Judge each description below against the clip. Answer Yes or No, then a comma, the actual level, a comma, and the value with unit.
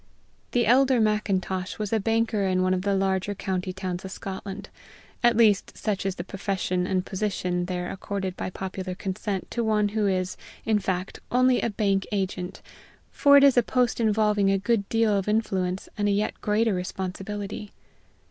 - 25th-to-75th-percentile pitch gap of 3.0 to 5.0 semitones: No, narrow, 2.4 semitones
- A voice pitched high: Yes, high, 200 Hz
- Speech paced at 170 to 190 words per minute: Yes, average, 175 wpm